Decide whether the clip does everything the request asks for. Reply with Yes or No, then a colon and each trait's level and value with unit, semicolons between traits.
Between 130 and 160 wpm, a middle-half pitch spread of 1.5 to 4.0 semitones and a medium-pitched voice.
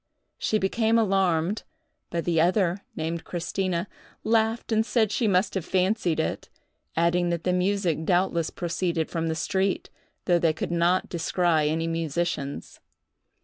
Yes: average, 145 wpm; average, 2.8 semitones; medium, 175 Hz